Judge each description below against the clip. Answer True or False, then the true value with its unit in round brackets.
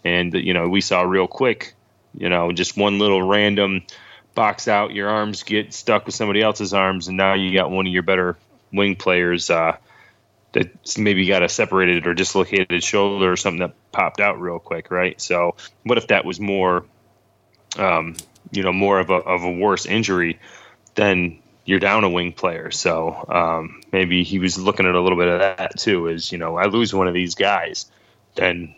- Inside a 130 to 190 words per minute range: False (200 wpm)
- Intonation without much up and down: True (2.1 semitones)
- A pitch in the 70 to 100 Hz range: True (95 Hz)